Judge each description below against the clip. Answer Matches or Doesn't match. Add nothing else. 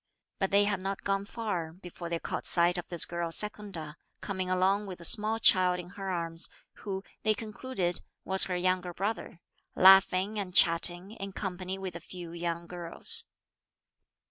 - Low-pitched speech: Doesn't match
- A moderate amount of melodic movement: Doesn't match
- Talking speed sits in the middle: Matches